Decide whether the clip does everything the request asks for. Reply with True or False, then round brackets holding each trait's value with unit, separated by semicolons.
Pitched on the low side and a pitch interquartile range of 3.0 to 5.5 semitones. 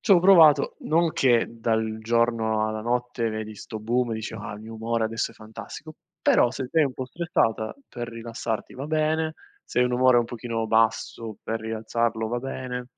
False (115 Hz; 2.5 semitones)